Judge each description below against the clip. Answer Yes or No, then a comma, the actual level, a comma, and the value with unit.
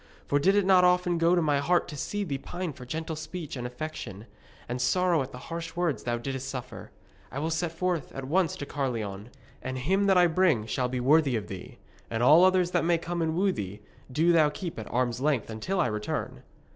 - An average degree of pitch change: No, wide, 5.7 semitones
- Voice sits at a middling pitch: Yes, medium, 155 Hz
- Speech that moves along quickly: Yes, fast, 225 wpm